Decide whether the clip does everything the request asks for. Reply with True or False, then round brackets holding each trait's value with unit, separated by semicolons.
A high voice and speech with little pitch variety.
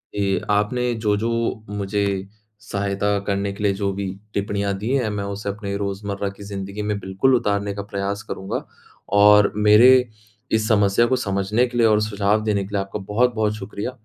False (100 Hz; 1.2 semitones)